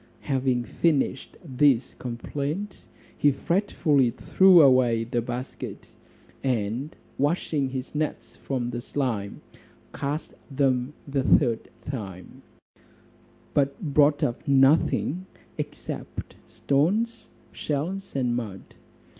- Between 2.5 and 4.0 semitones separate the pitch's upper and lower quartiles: Yes, average, 3.4 semitones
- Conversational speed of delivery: No, slow, 95 wpm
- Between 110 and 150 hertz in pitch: Yes, low, 135 Hz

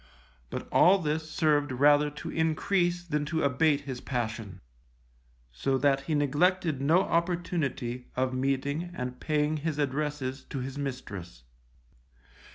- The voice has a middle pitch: Yes, medium, 145 Hz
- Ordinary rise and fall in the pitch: Yes, average, 3.5 semitones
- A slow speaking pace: Yes, slow, 130 wpm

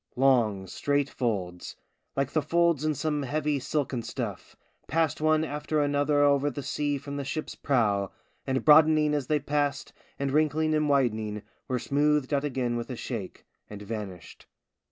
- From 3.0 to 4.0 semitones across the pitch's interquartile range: Yes, average, 3.7 semitones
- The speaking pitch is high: No, medium, 140 Hz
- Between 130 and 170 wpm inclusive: Yes, average, 160 wpm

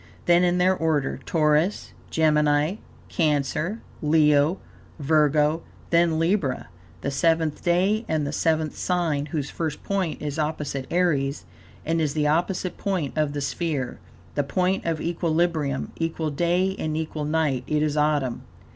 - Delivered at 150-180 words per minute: No, average, 140 wpm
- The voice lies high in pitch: No, medium, 155 Hz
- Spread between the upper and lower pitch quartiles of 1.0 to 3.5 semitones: Yes, narrow, 2.6 semitones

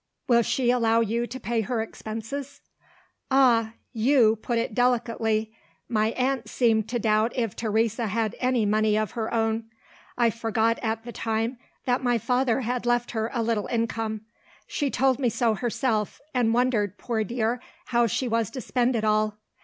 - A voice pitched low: No, high, 230 Hz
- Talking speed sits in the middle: Yes, average, 170 wpm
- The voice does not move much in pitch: Yes, narrow, 1.9 semitones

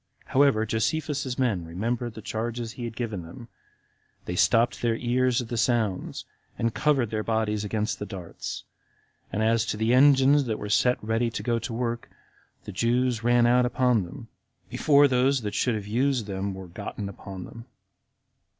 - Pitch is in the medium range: No, low, 115 Hz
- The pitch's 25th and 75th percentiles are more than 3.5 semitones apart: No, average, 2.7 semitones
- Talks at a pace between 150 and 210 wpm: Yes, average, 175 wpm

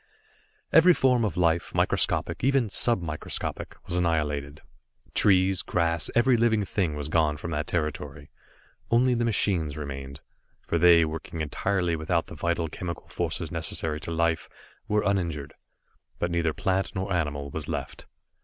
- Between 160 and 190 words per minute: No, average, 145 wpm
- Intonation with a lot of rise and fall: No, average, 4.1 semitones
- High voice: No, very low, 85 Hz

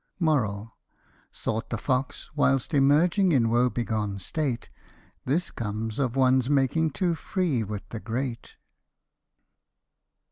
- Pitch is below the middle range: Yes, low, 130 Hz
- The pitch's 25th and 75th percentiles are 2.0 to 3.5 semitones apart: No, average, 4.3 semitones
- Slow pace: Yes, slow, 115 wpm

